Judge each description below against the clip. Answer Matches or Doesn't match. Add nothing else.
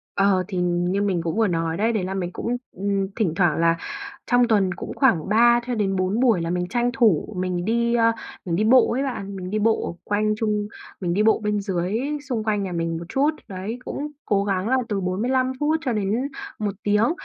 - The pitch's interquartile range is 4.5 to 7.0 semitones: Doesn't match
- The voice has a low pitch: Doesn't match